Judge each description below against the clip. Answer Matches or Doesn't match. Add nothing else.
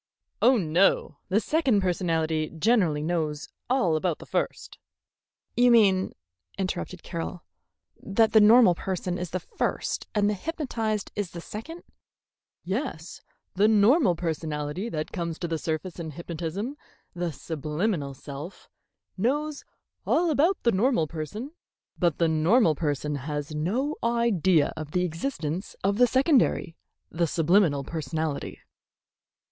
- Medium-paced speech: Doesn't match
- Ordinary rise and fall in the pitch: Doesn't match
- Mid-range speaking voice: Matches